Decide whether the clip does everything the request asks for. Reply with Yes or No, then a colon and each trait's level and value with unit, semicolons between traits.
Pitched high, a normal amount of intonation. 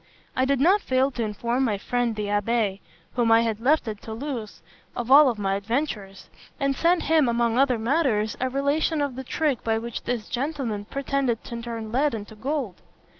Yes: high, 240 Hz; average, 4.0 semitones